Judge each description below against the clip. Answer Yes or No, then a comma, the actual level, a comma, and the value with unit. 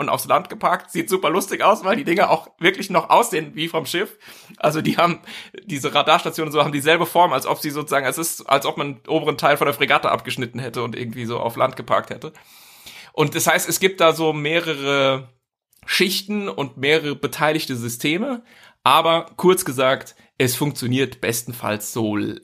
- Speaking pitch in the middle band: Yes, medium, 150 Hz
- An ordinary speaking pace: No, fast, 195 wpm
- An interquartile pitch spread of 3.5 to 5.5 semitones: Yes, average, 4.0 semitones